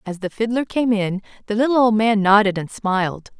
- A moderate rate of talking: No, fast, 210 wpm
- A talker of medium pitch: No, high, 215 Hz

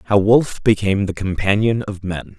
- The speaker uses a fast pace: No, average, 175 wpm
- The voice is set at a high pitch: No, low, 100 Hz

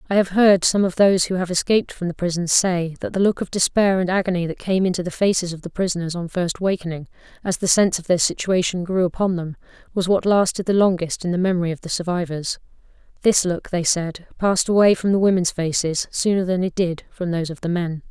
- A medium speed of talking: No, fast, 230 wpm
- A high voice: No, medium, 180 Hz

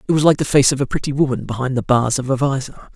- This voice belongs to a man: Yes, male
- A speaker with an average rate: No, fast, 305 wpm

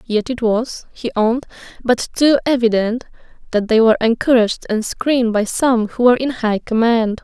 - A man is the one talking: No, female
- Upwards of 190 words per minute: No, average, 175 wpm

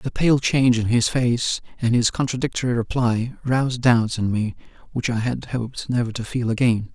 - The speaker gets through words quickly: No, average, 190 wpm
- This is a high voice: No, low, 120 Hz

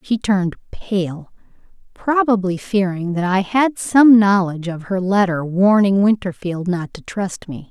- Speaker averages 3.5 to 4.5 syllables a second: Yes, 4.2 syllables/s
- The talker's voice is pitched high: Yes, high, 195 Hz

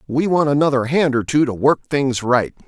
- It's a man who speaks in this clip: Yes, male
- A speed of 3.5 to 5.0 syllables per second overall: No, 5.2 syllables/s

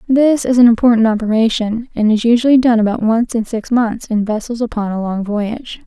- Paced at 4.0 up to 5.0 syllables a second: No, 5.5 syllables/s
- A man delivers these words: No, female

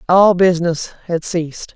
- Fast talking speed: No, slow, 135 wpm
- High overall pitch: No, medium, 170 Hz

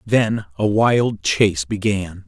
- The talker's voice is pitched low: Yes, low, 100 Hz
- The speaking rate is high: No, slow, 130 wpm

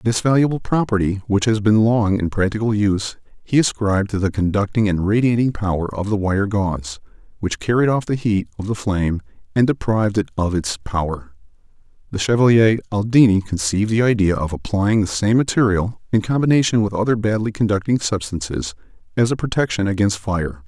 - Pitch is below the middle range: Yes, low, 105 Hz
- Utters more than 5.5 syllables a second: Yes, 5.7 syllables/s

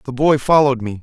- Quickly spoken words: Yes, fast, 235 wpm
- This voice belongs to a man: Yes, male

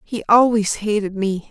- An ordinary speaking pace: Yes, average, 160 wpm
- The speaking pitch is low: No, high, 210 Hz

